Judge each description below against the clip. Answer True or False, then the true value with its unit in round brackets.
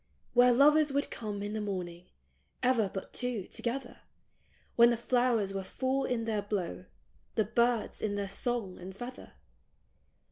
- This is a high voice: True (225 Hz)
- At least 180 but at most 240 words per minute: False (165 wpm)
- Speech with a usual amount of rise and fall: True (3.8 semitones)